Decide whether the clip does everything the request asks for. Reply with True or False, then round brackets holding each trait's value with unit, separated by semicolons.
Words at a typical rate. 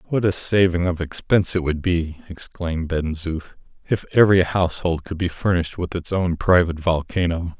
True (175 wpm)